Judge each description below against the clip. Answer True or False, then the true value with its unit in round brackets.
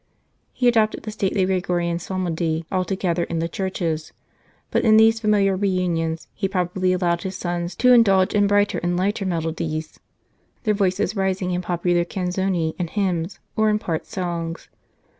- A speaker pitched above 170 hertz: True (185 Hz)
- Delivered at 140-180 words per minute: True (155 wpm)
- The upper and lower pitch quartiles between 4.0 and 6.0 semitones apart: False (2.4 semitones)